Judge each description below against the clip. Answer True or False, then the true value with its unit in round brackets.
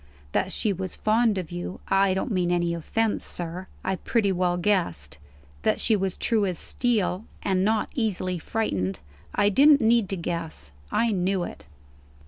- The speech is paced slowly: False (165 wpm)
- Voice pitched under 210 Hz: True (190 Hz)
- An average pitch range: True (3.5 semitones)